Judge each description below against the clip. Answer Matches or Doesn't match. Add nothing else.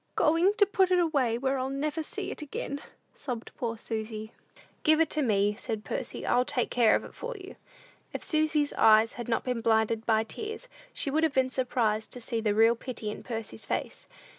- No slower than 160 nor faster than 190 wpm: Doesn't match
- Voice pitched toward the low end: Doesn't match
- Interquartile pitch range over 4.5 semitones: Matches